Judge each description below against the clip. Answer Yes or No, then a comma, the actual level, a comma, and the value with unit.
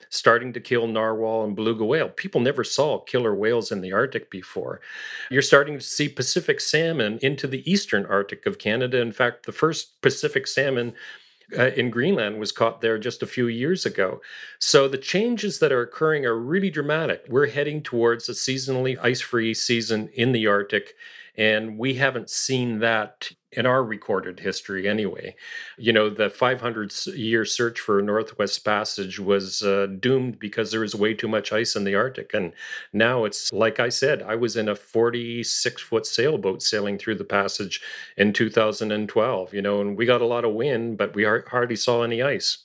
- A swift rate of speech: No, average, 185 wpm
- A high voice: No, low, 115 Hz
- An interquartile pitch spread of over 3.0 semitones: Yes, average, 3.4 semitones